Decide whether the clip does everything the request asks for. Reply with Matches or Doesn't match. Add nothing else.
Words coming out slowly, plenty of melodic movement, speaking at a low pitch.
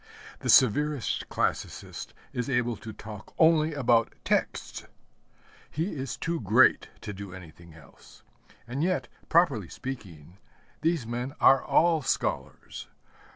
Matches